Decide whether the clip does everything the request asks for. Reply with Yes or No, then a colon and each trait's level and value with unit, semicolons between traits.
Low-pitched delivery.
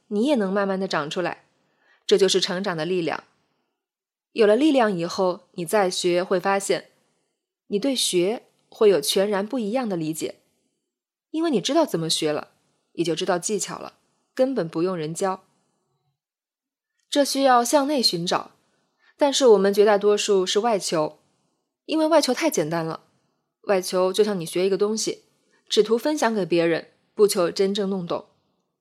No: high, 200 Hz